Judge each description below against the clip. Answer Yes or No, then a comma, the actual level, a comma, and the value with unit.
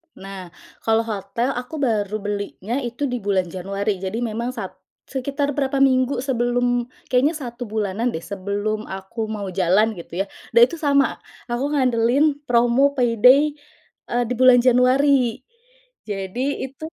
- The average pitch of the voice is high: Yes, high, 240 Hz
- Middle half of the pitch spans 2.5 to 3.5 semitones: No, average, 4.0 semitones